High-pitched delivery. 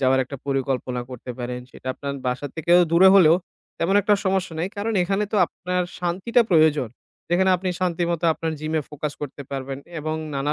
No: medium, 160 Hz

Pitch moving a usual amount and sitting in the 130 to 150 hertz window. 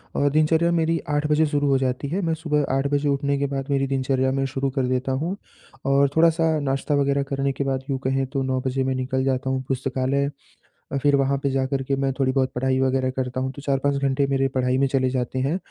No: narrow, 1.3 semitones; low, 135 Hz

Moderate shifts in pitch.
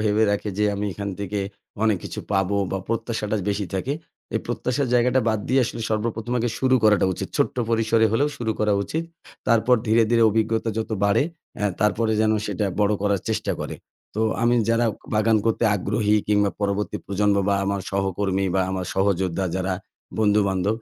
No: narrow, 2.3 semitones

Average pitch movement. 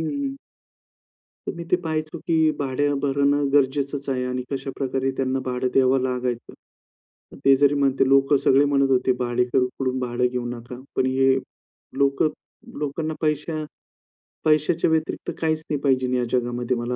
No: narrow, 2.3 semitones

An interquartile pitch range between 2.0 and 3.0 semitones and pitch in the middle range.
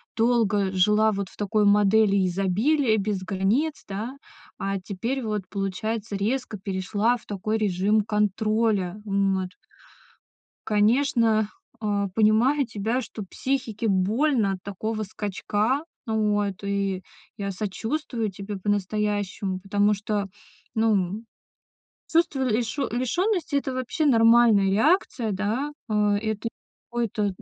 No: narrow, 2.6 semitones; high, 210 Hz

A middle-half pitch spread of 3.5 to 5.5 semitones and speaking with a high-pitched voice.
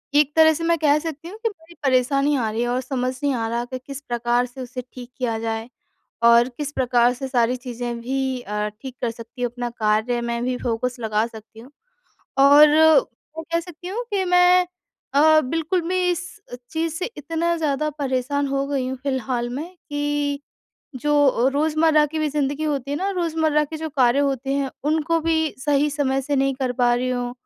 Yes: average, 4.0 semitones; very high, 275 Hz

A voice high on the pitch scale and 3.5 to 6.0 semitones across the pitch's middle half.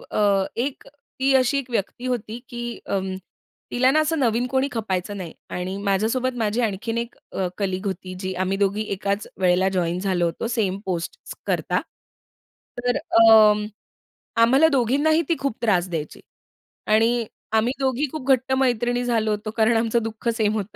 Yes: high, 225 Hz; average, 4.0 semitones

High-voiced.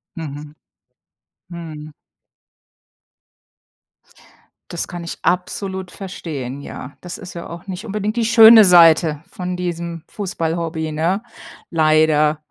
No: medium, 170 Hz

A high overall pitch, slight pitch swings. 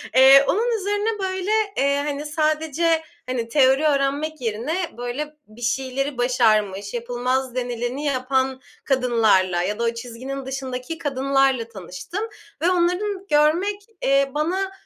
No: very high, 270 Hz; average, 4.3 semitones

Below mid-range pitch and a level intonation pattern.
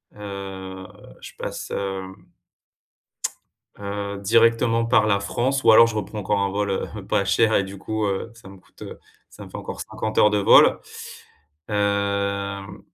Yes: low, 100 Hz; narrow, 1.8 semitones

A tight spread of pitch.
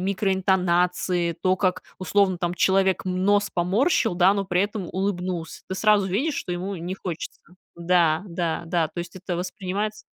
Yes: narrow, 1.9 semitones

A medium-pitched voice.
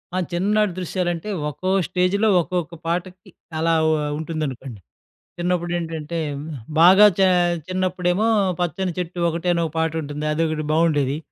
Yes: medium, 170 Hz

